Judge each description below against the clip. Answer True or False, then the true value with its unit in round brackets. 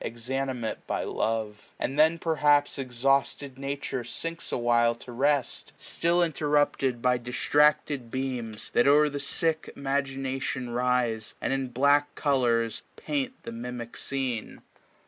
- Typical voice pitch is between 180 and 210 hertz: False (135 Hz)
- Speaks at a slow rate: True (130 wpm)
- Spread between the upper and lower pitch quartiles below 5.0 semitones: True (3.2 semitones)